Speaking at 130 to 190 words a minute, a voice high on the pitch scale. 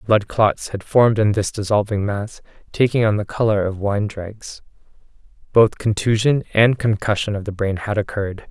No: average, 170 wpm; low, 105 Hz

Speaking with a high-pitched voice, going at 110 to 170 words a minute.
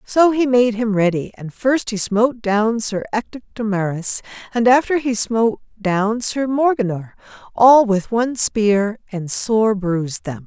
Yes: high, 220 Hz; average, 165 wpm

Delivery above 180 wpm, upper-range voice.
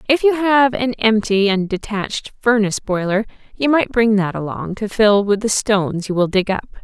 Yes: average, 200 wpm; high, 215 Hz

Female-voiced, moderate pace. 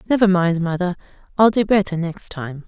Yes: female; average, 180 wpm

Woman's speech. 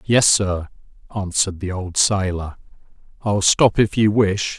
No: male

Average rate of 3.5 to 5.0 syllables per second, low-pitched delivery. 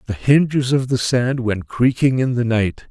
Yes: 4.5 syllables/s; low, 125 Hz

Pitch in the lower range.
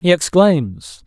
No: medium, 155 Hz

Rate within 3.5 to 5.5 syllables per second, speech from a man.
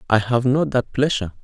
No: 5.9 syllables/s; male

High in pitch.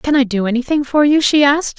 Yes: very high, 275 Hz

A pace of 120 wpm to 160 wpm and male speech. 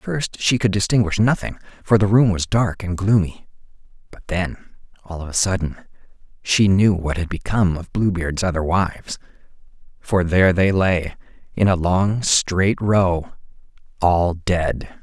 Yes: average, 155 wpm; male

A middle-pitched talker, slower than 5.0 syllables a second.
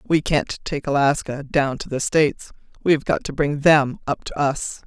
Yes: medium, 145 Hz; 4.7 syllables/s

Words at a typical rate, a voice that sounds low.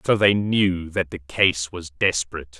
Yes: average, 185 wpm; very low, 85 Hz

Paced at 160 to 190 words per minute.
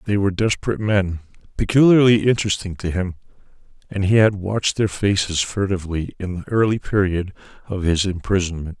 No: average, 150 wpm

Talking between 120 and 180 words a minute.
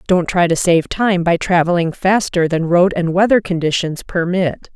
Yes: average, 175 wpm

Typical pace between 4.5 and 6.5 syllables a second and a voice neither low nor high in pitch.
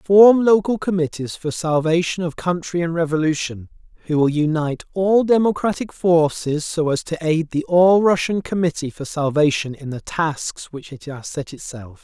Yes: 4.7 syllables/s; medium, 165 Hz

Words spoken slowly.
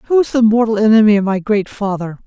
No: fast, 240 wpm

